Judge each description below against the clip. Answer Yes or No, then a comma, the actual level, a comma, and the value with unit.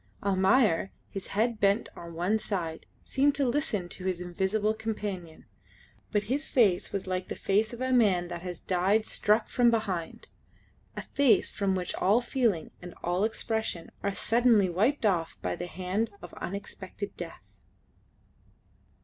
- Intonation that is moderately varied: Yes, average, 3.8 semitones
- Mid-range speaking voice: No, high, 200 Hz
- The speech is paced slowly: No, average, 155 wpm